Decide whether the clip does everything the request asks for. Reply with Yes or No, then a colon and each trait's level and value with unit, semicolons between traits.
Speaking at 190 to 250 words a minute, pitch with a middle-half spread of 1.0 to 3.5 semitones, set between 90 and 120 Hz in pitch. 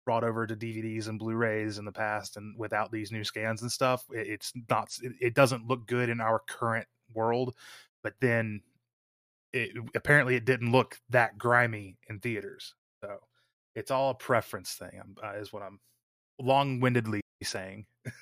No: average, 170 wpm; narrow, 2.6 semitones; low, 115 Hz